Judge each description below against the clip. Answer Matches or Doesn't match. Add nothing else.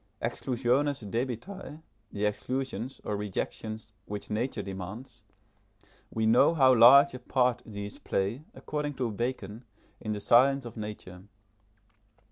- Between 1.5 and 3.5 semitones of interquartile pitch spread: Doesn't match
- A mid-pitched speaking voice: Doesn't match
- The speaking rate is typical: Doesn't match